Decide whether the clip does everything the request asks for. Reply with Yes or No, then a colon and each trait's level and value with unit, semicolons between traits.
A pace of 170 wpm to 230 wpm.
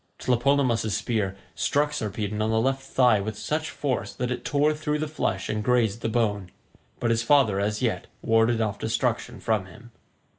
Yes: average, 180 wpm